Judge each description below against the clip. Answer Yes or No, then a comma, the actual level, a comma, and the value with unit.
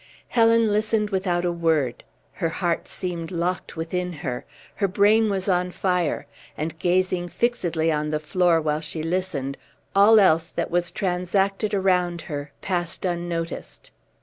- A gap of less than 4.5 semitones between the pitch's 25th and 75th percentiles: Yes, average, 2.7 semitones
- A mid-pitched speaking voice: Yes, medium, 175 Hz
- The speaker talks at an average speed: Yes, average, 145 wpm